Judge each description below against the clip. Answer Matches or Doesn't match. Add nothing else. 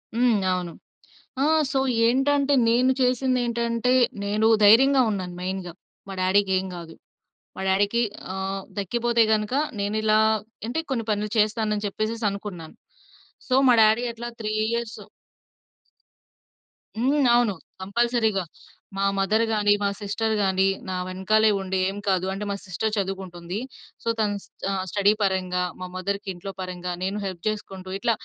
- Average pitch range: Matches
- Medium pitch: Doesn't match